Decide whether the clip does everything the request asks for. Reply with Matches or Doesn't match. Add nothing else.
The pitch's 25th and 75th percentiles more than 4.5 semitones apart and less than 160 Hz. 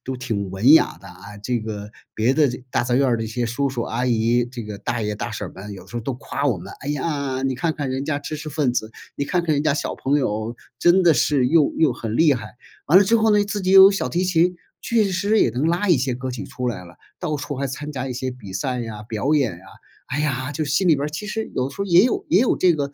Matches